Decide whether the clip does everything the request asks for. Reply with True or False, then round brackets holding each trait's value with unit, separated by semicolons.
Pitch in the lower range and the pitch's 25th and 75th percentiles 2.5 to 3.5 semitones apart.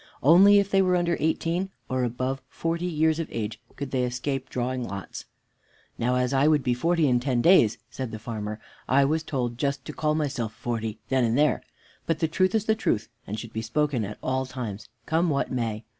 False (130 Hz; 5.1 semitones)